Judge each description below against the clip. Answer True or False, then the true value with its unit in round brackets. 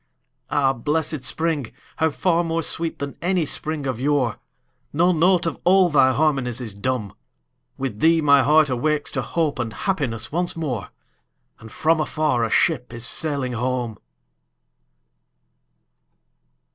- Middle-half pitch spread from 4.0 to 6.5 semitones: True (4.5 semitones)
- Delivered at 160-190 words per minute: False (135 wpm)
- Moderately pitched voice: True (145 Hz)